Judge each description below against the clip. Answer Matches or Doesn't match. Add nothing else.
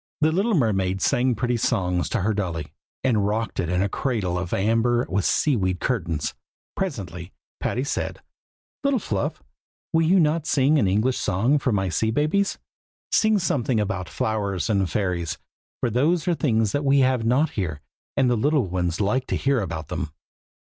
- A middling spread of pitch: Doesn't match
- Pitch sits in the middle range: Doesn't match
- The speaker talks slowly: Doesn't match